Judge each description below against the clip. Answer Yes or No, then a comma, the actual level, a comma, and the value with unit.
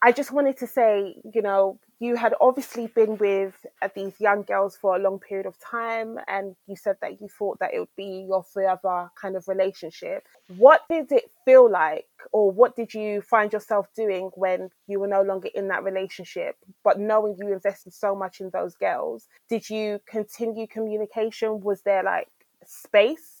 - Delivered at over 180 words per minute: Yes, average, 190 wpm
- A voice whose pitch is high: Yes, high, 205 Hz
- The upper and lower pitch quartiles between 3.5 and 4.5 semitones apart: No, average, 2.7 semitones